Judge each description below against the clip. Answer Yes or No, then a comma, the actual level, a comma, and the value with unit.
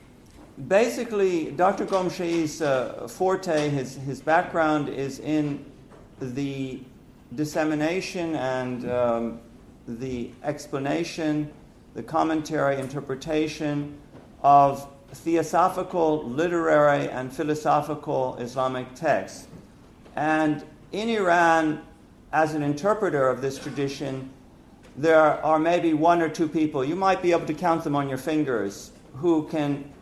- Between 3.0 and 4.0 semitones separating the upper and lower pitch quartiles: Yes, average, 3.3 semitones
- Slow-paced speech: Yes, slow, 110 wpm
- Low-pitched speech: No, medium, 150 Hz